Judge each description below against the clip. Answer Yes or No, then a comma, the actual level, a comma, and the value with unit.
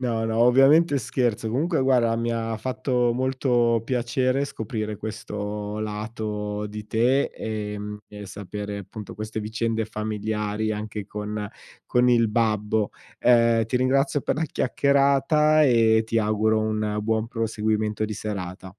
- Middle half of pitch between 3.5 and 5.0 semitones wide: No, average, 2.7 semitones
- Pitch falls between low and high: No, low, 110 Hz